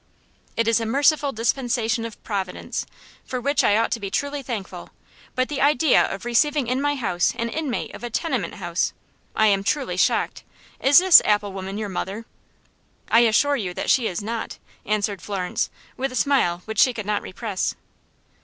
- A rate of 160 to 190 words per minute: Yes, average, 180 wpm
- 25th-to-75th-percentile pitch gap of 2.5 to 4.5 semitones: No, average, 4.9 semitones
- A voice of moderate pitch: No, high, 230 Hz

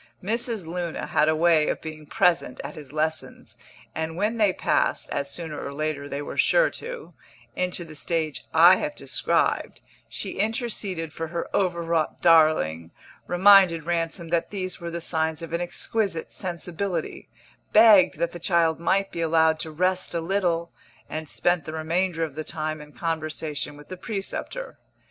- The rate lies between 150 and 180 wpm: Yes, average, 165 wpm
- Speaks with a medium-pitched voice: Yes, medium, 170 Hz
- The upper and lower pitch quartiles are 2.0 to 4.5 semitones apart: Yes, average, 2.8 semitones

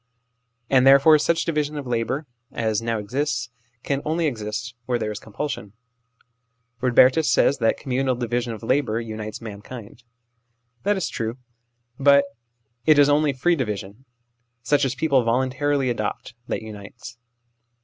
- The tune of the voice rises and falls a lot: No, average, 4.0 semitones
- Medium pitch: No, low, 125 Hz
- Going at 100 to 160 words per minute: Yes, average, 140 wpm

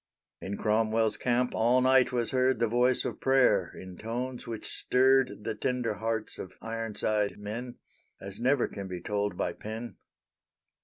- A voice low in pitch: Yes, low, 115 Hz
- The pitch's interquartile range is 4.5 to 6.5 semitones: No, average, 3.0 semitones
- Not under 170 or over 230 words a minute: No, average, 155 wpm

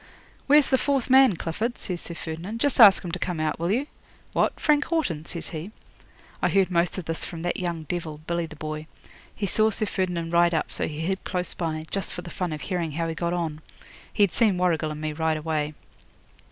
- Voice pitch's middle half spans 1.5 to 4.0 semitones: Yes, average, 3.5 semitones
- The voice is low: No, medium, 170 Hz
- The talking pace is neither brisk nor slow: No, fast, 220 wpm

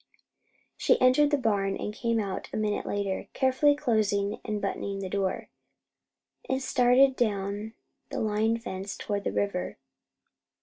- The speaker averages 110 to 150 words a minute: Yes, average, 140 wpm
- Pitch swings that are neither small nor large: Yes, average, 4.0 semitones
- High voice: Yes, high, 215 Hz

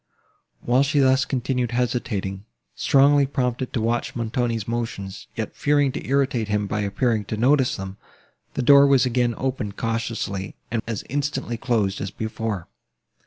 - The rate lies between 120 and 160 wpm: Yes, average, 150 wpm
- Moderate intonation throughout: Yes, average, 3.5 semitones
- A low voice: Yes, low, 120 Hz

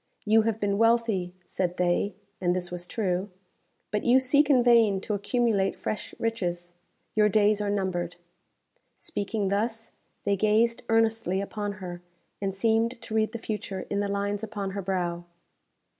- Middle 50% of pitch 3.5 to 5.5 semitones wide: No, average, 3.0 semitones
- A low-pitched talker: No, high, 205 Hz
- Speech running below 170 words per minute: Yes, average, 160 wpm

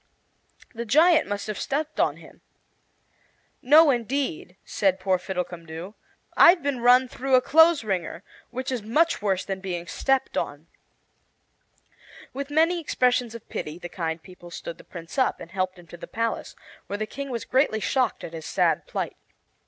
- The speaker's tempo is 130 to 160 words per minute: No, average, 170 wpm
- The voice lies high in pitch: Yes, high, 225 Hz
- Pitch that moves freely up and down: Yes, wide, 6.9 semitones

